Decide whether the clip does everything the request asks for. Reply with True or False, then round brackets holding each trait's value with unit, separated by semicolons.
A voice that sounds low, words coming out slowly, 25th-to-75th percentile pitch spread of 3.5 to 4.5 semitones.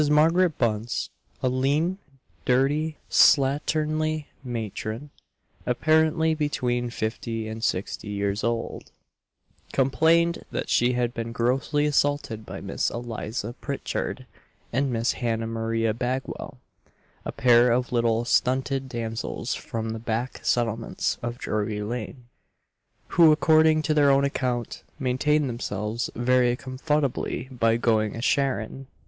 True (125 Hz; 120 wpm; 4.1 semitones)